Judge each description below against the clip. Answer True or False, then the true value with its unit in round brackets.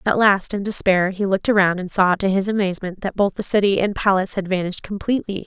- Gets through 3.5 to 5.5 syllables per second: False (6.4 syllables/s)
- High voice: True (195 Hz)